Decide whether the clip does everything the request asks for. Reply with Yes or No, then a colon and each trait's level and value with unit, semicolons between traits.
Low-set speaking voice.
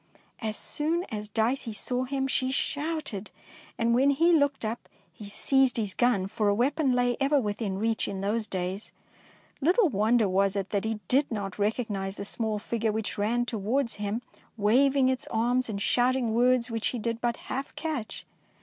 No: high, 230 Hz